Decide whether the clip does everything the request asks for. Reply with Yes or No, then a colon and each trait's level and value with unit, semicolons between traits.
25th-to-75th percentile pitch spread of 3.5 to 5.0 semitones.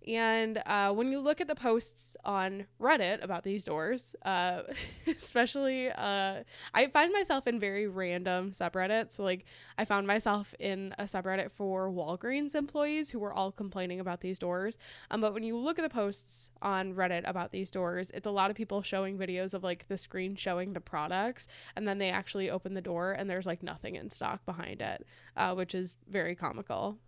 No: average, 3.1 semitones